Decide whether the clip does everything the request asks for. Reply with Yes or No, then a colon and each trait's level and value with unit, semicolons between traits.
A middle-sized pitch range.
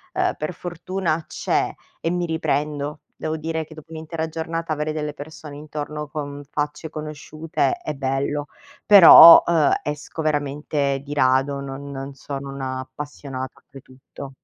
No: narrow, 2.2 semitones